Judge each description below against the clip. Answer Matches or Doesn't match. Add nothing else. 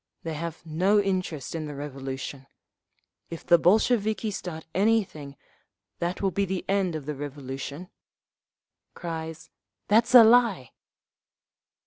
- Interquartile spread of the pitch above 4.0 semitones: Matches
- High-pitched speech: Doesn't match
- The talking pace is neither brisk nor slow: Doesn't match